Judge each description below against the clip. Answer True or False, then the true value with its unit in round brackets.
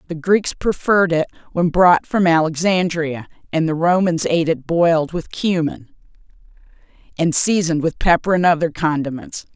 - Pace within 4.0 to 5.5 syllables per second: True (5.0 syllables/s)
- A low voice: False (165 Hz)